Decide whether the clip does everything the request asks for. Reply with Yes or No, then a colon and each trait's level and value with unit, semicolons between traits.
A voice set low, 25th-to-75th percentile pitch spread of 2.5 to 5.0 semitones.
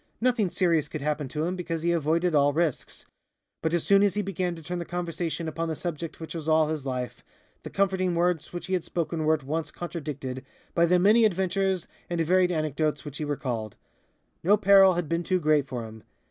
No: medium, 165 Hz; average, 2.9 semitones